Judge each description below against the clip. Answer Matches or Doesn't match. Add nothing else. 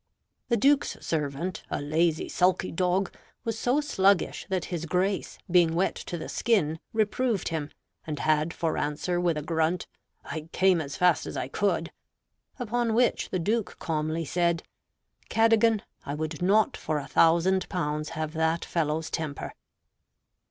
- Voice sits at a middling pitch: Matches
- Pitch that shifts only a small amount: Doesn't match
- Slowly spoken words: Doesn't match